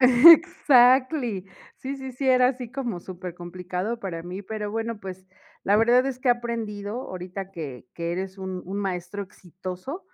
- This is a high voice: Yes, high, 205 Hz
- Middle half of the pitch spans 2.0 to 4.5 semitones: No, average, 5.2 semitones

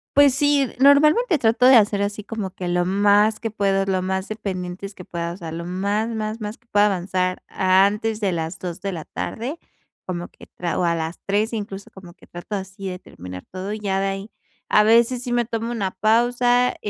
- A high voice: Yes, high, 200 Hz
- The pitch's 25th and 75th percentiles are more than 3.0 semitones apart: Yes, average, 3.4 semitones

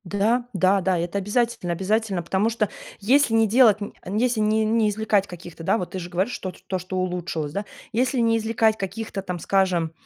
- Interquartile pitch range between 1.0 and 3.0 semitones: No, average, 3.5 semitones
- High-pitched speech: Yes, high, 200 Hz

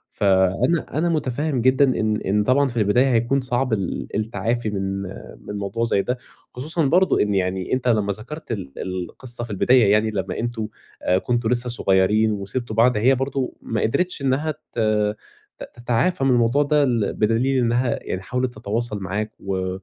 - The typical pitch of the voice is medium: No, low, 115 Hz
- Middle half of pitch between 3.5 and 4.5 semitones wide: Yes, average, 4.0 semitones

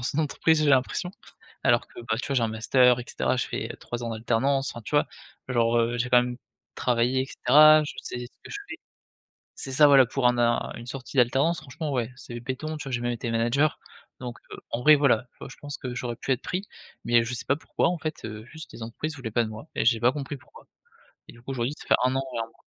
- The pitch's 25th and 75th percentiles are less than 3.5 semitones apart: Yes, average, 3.0 semitones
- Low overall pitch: Yes, low, 125 Hz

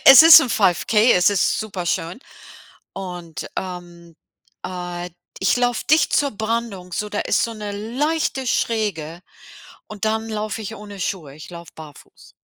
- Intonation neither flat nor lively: Yes, average, 4.1 semitones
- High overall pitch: Yes, high, 205 Hz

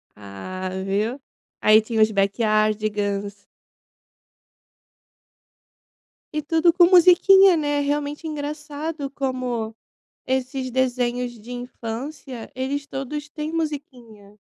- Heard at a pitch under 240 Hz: No, very high, 260 Hz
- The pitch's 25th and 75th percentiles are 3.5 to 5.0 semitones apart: No, wide, 5.4 semitones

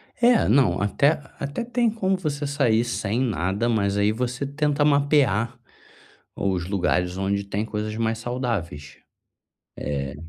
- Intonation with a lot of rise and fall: Yes, wide, 6.1 semitones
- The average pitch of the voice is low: Yes, low, 115 Hz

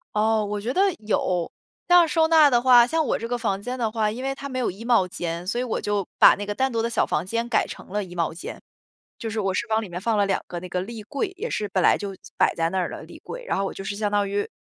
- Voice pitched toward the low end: No, high, 215 Hz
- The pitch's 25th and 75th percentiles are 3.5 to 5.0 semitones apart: Yes, average, 4.1 semitones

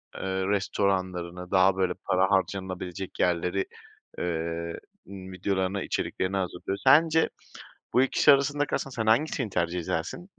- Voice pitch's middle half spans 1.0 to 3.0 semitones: Yes, narrow, 2.5 semitones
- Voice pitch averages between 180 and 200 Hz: No, very low, 95 Hz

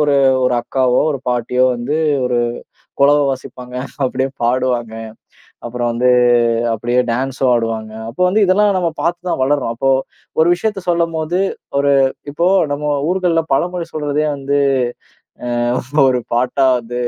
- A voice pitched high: No, low, 135 Hz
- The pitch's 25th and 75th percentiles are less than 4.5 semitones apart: No, average, 4.8 semitones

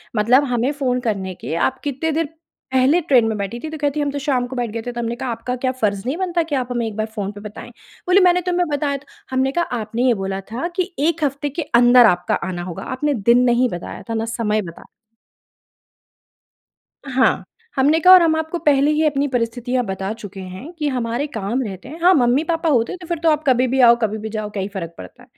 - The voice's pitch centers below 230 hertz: No, very high, 255 Hz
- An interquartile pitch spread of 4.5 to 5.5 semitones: Yes, average, 5.1 semitones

